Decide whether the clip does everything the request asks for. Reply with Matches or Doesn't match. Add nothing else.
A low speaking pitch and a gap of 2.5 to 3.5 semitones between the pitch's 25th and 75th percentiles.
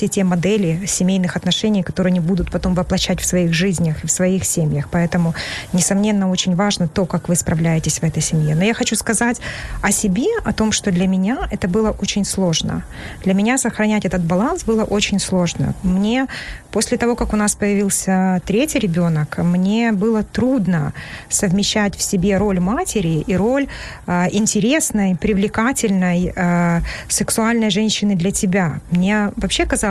Doesn't match